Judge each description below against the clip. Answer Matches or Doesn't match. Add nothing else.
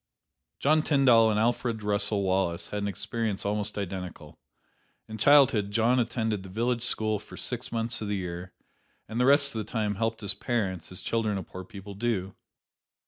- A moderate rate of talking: Matches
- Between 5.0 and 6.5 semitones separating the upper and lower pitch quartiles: Doesn't match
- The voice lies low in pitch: Matches